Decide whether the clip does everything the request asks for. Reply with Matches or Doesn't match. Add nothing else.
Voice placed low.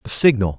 Matches